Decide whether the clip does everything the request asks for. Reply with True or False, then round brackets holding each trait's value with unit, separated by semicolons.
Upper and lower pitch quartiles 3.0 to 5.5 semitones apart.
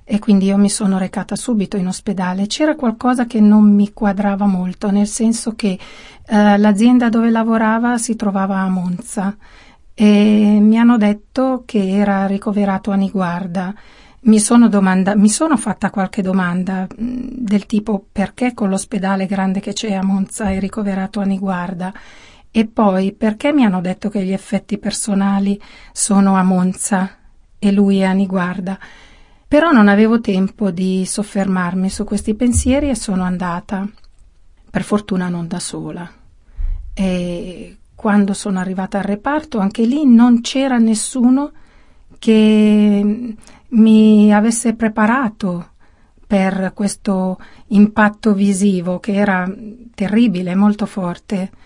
False (2.5 semitones)